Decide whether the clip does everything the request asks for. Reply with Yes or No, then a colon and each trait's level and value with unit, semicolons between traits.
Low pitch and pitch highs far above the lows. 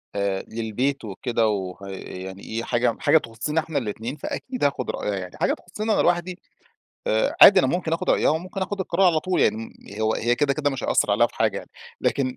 Yes: low, 120 Hz; wide, 7.0 semitones